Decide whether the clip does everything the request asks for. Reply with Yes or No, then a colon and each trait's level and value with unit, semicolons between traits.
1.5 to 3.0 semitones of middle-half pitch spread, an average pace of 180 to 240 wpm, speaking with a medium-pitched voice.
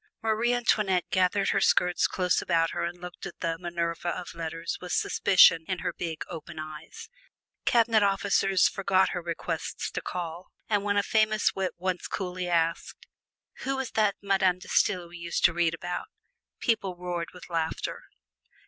No: average, 2.7 semitones; average, 165 wpm; medium, 180 Hz